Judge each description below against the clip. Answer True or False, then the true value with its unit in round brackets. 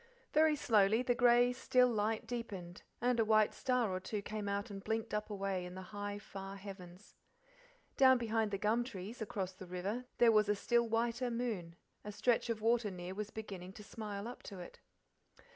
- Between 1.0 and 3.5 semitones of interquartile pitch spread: True (3.2 semitones)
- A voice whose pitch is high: True (215 Hz)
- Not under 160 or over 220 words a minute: True (195 wpm)